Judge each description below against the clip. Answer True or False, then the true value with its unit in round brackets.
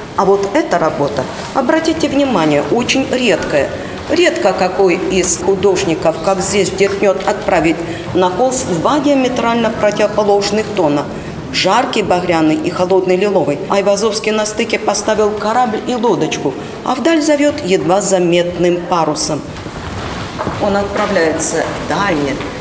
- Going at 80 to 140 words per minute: True (115 wpm)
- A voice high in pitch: True (200 Hz)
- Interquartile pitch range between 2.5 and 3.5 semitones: False (4.2 semitones)